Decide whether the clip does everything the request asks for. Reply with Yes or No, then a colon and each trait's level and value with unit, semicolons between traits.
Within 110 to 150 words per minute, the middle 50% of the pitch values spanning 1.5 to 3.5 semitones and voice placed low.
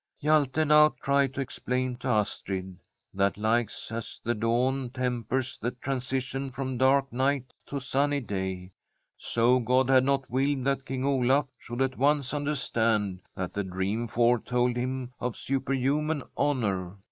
Yes: average, 145 wpm; average, 2.8 semitones; low, 130 Hz